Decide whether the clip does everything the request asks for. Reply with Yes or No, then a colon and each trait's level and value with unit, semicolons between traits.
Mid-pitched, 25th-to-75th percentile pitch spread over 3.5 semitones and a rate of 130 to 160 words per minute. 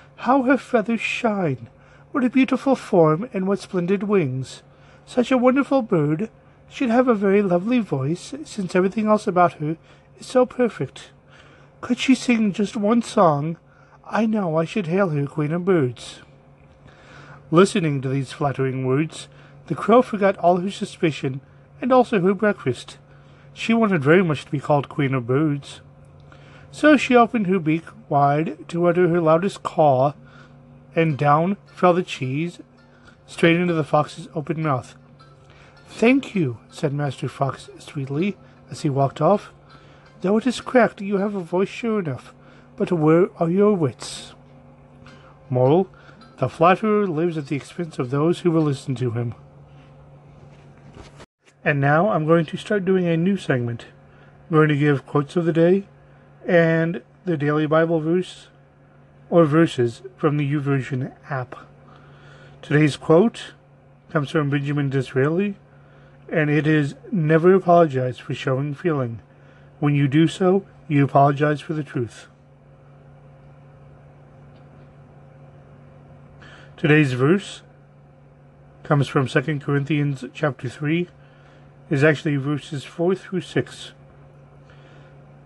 Yes: medium, 150 Hz; average, 4.9 semitones; average, 140 wpm